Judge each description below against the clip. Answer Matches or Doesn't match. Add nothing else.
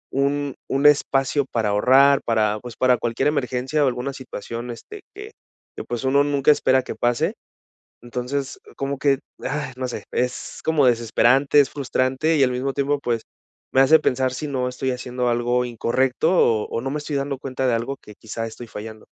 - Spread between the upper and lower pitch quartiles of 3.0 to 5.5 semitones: Doesn't match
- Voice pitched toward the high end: Doesn't match